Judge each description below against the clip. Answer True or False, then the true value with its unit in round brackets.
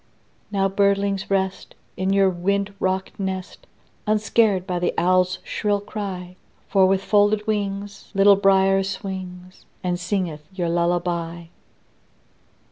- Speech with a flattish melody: True (1.7 semitones)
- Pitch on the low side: False (190 Hz)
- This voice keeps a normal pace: False (120 wpm)